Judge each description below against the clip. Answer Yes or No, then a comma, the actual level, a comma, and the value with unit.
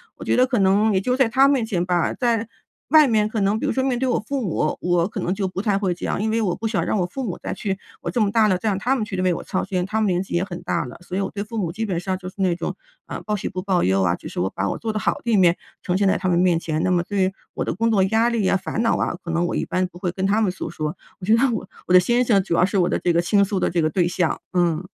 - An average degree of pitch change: Yes, average, 3.7 semitones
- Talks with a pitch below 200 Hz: Yes, high, 190 Hz